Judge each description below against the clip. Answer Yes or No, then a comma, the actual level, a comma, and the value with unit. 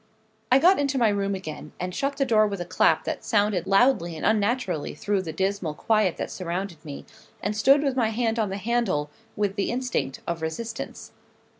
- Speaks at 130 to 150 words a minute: No, average, 195 wpm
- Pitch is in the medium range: No, high, 205 Hz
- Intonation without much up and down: No, average, 4.7 semitones